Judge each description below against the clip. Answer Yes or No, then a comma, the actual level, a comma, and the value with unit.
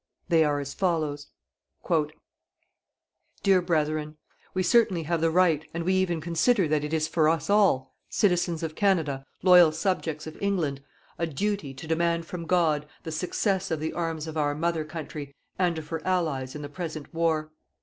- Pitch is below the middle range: No, medium, 160 Hz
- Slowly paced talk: No, average, 170 wpm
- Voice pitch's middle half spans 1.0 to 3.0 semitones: Yes, narrow, 2.6 semitones